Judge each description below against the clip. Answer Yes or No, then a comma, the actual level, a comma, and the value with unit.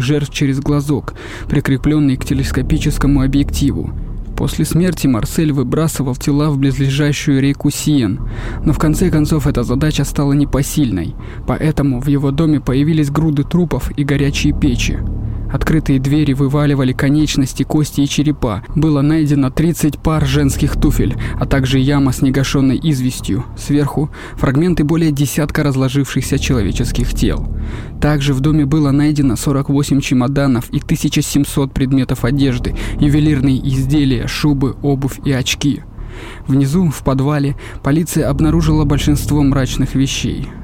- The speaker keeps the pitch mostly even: Yes, narrow, 1.9 semitones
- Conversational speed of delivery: Yes, average, 125 wpm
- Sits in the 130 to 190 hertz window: Yes, medium, 140 Hz